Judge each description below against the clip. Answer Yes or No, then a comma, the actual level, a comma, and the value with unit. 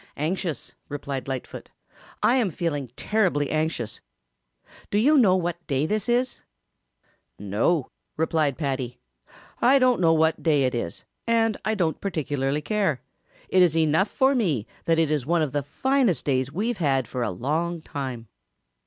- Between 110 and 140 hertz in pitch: No, medium, 160 Hz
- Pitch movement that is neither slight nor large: No, wide, 6.3 semitones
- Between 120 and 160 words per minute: Yes, average, 155 wpm